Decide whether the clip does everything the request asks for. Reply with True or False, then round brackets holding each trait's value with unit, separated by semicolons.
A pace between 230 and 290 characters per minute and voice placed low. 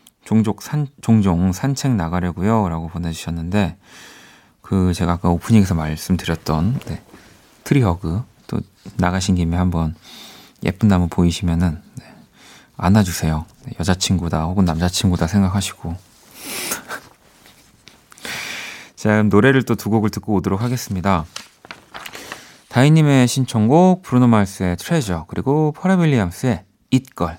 True (280 characters per minute; 95 Hz)